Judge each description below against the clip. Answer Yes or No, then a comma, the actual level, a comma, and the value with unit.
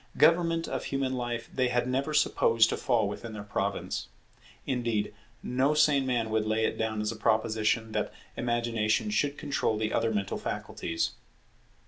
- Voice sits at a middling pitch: No, low, 115 Hz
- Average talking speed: Yes, average, 160 wpm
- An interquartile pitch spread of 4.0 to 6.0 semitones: No, average, 3.3 semitones